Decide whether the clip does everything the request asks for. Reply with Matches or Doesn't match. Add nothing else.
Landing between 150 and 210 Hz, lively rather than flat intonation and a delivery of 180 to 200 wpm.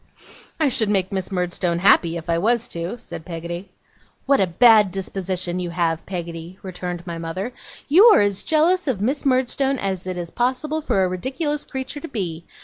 Matches